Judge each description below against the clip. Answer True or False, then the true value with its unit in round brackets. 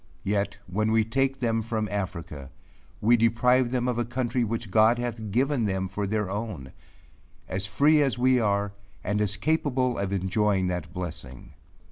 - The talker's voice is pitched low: True (110 Hz)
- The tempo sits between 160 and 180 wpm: True (165 wpm)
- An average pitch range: True (3.7 semitones)